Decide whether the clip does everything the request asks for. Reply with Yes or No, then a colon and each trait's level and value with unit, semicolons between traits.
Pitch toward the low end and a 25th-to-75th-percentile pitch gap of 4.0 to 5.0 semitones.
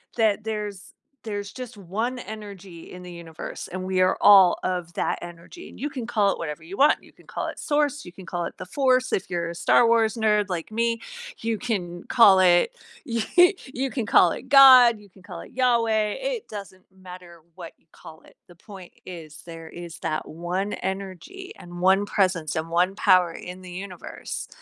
No: high, 195 Hz; average, 4.4 semitones